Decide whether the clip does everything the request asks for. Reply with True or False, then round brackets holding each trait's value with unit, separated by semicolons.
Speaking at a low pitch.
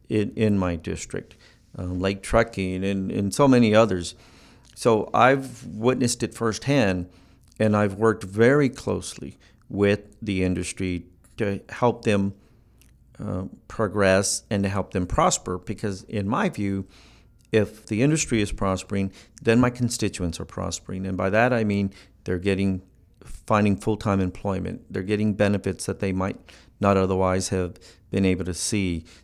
True (100 Hz)